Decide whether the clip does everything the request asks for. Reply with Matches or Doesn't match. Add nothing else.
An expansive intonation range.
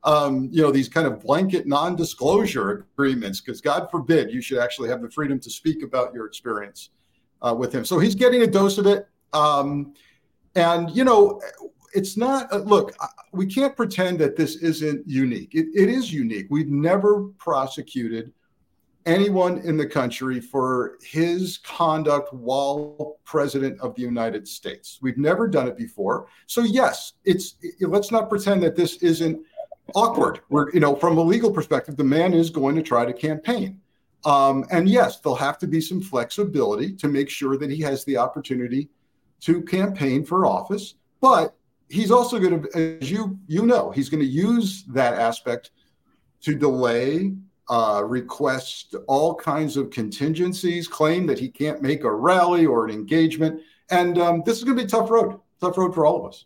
Matches